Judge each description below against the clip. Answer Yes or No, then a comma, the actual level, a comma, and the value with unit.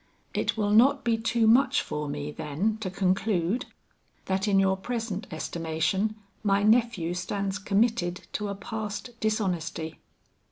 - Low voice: No, high, 200 Hz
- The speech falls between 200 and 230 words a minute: No, slow, 135 wpm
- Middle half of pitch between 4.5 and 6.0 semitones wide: No, average, 3.7 semitones